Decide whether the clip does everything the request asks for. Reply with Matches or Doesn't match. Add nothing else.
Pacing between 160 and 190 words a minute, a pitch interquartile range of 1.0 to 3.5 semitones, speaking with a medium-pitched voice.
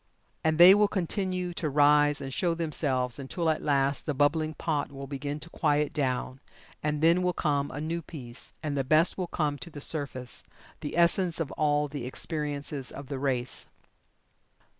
Matches